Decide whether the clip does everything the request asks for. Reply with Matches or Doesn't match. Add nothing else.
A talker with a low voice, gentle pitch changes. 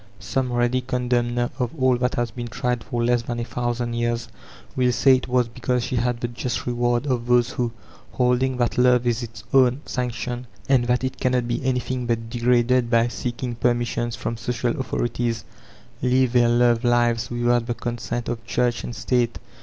Matches